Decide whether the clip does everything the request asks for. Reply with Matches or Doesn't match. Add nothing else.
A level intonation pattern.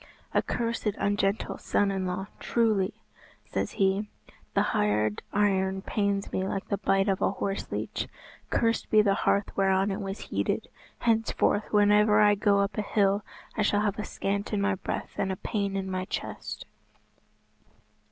Matches